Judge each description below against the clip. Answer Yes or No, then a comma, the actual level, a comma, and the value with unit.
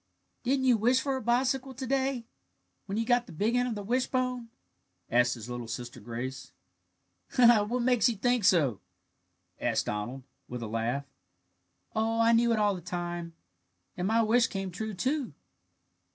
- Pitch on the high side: Yes, high, 220 Hz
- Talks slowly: No, average, 165 wpm